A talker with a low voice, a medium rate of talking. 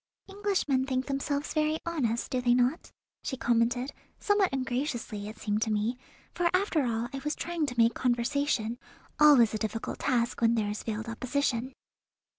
No: very high, 250 Hz; average, 165 wpm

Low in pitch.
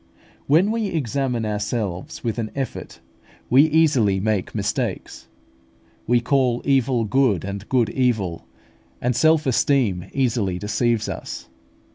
Yes: low, 120 Hz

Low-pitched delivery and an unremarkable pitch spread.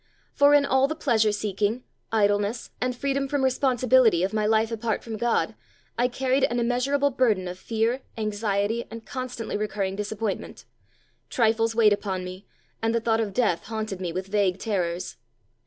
No: high, 225 Hz; average, 3.4 semitones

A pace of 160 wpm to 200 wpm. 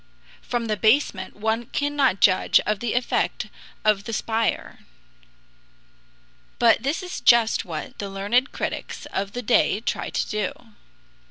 No: average, 140 wpm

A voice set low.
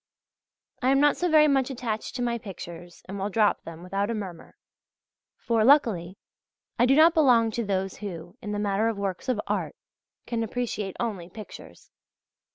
No: high, 215 Hz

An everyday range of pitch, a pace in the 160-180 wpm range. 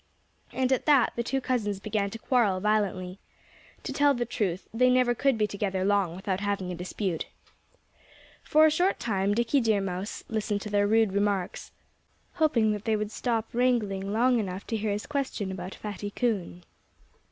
Yes: average, 3.7 semitones; average, 175 wpm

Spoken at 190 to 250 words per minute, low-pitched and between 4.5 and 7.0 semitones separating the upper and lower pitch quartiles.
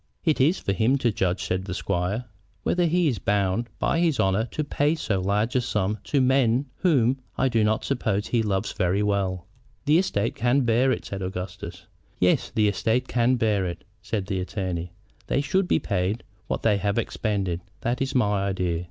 Yes: average, 195 wpm; low, 110 Hz; average, 5.0 semitones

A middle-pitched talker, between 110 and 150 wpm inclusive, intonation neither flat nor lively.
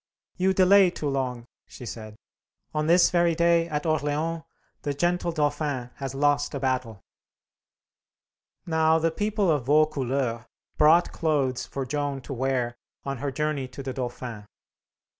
Yes: medium, 145 Hz; average, 140 wpm; average, 3.8 semitones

